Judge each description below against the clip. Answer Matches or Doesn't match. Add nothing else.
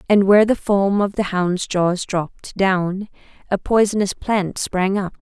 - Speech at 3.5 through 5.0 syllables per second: Matches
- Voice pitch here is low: Doesn't match